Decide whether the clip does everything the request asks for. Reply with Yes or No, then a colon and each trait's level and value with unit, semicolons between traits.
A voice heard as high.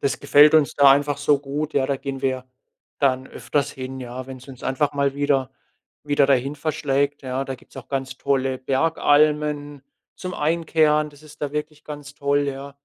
No: medium, 140 Hz